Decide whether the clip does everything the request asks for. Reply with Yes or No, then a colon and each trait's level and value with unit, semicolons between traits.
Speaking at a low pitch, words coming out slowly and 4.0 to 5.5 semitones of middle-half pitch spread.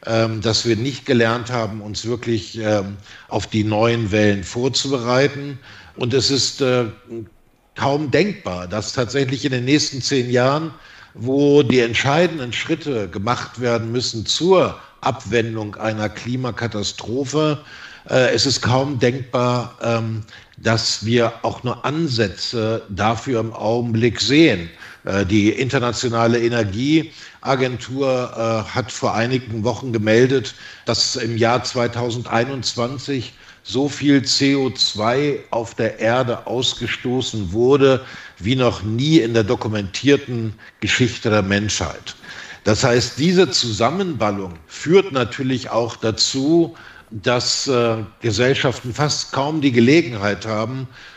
No: low, 120 Hz; slow, 115 wpm; average, 3.2 semitones